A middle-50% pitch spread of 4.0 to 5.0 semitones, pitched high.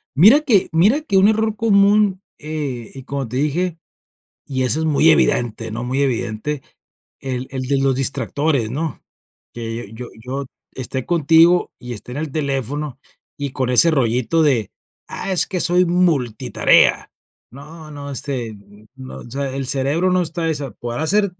No: average, 4.7 semitones; medium, 140 Hz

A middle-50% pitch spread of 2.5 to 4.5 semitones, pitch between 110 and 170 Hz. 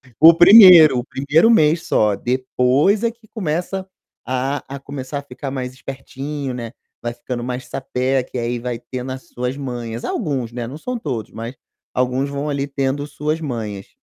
Yes: average, 3.2 semitones; low, 135 Hz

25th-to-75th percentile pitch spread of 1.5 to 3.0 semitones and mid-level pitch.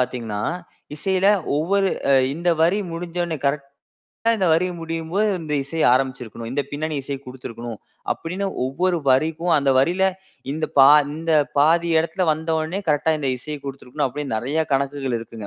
No: average, 3.8 semitones; medium, 150 Hz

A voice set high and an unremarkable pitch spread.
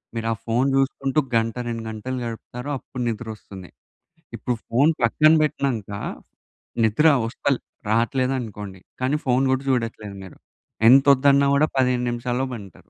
No: low, 125 Hz; average, 3.0 semitones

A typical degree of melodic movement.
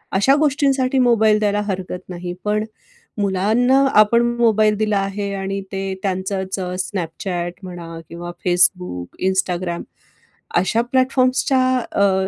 Yes: average, 3.8 semitones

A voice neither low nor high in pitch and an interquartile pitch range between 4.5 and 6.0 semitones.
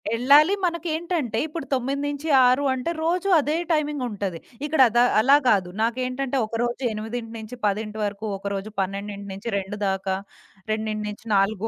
No: high, 235 Hz; average, 5.3 semitones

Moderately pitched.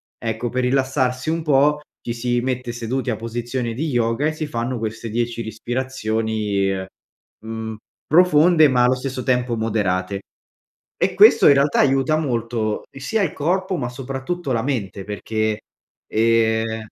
No: low, 120 Hz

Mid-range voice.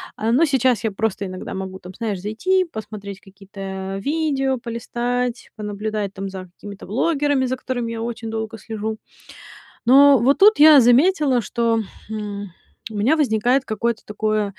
No: high, 225 Hz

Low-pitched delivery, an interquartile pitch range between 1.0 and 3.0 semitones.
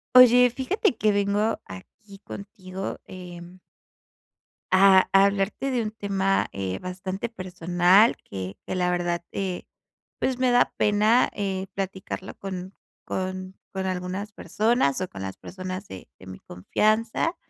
No: high, 190 Hz; average, 2.7 semitones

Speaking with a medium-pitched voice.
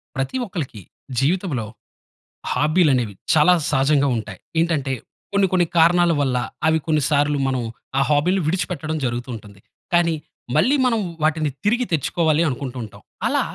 Yes: medium, 155 Hz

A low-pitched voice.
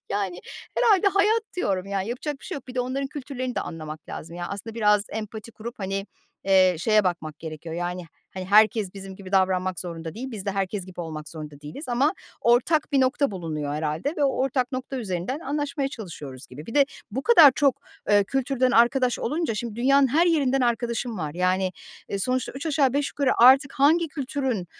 No: high, 230 Hz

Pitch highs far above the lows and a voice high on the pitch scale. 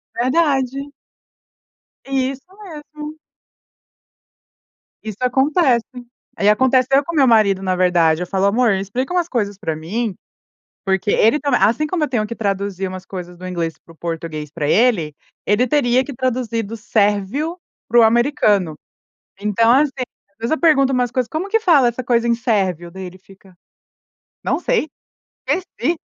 Yes: wide, 5.9 semitones; high, 230 Hz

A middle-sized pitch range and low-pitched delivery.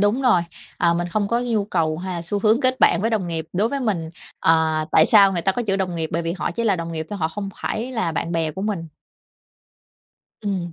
No: average, 4.4 semitones; medium, 185 Hz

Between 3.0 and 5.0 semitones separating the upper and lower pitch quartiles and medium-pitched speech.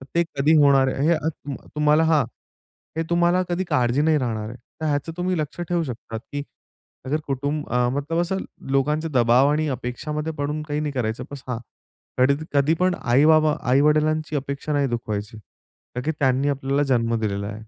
Yes: average, 3.5 semitones; medium, 145 Hz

